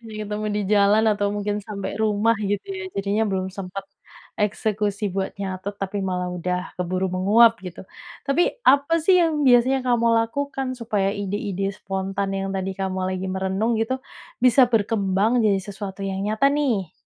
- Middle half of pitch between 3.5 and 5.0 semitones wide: No, average, 3.1 semitones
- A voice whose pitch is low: No, high, 205 Hz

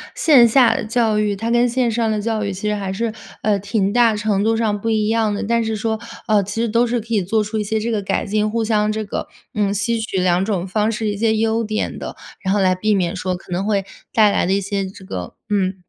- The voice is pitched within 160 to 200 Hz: No, high, 215 Hz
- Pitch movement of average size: No, narrow, 2.1 semitones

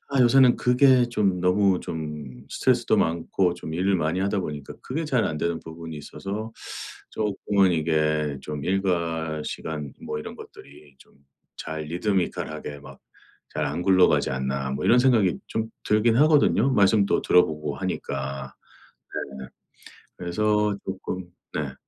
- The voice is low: Yes, very low, 90 Hz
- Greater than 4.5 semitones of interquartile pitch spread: Yes, wide, 5.5 semitones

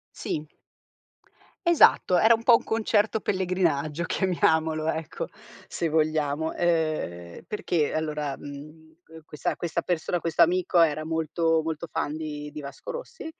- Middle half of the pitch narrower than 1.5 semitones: No, narrow, 2.5 semitones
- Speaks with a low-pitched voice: No, medium, 160 Hz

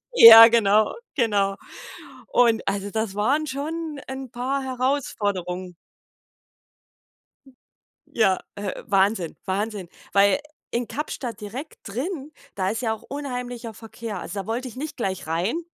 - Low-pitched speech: No, high, 225 Hz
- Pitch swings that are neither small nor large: Yes, average, 4.6 semitones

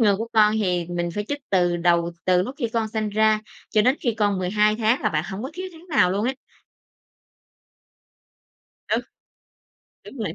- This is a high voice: Yes, high, 210 Hz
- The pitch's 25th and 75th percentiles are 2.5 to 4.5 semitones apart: Yes, average, 3.8 semitones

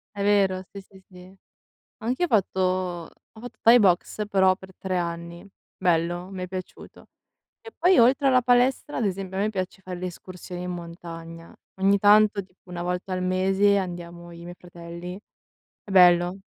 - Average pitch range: No, narrow, 2.3 semitones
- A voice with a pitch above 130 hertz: Yes, medium, 185 Hz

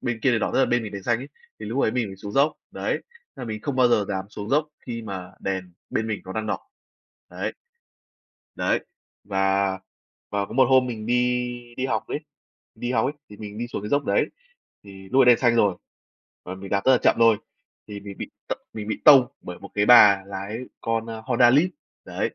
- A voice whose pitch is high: No, low, 110 Hz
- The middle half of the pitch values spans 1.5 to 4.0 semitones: Yes, average, 3.6 semitones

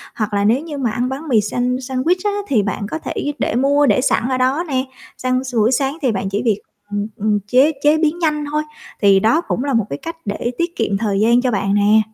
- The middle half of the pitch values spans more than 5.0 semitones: Yes, wide, 5.4 semitones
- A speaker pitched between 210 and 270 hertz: Yes, very high, 250 Hz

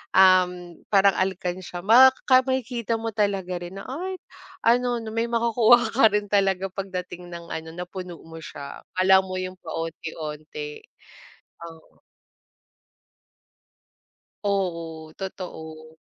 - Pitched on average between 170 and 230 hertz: Yes, medium, 185 Hz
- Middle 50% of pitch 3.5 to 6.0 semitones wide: Yes, average, 4.3 semitones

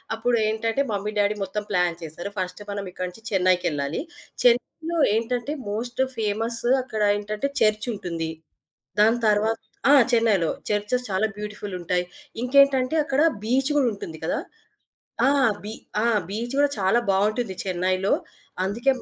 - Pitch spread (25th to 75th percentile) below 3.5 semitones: No, average, 4.1 semitones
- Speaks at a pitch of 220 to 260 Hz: No, high, 210 Hz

